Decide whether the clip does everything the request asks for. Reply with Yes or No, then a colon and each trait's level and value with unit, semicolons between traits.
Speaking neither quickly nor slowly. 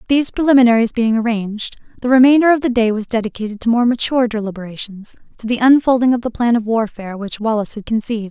Yes: average, 190 wpm